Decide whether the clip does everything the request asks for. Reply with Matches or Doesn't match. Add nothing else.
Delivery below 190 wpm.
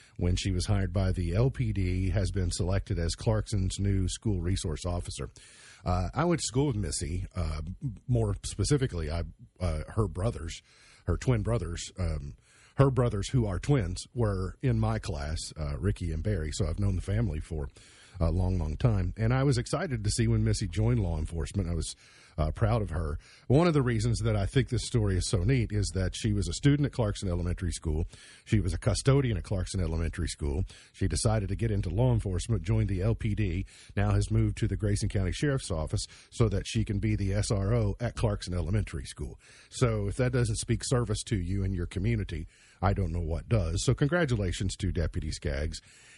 Doesn't match